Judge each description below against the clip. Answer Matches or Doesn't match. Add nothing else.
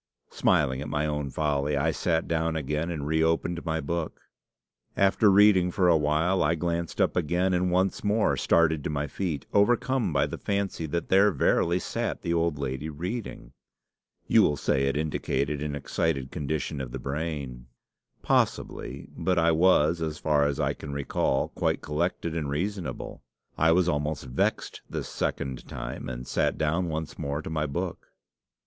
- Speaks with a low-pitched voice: Matches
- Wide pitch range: Doesn't match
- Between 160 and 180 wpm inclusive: Matches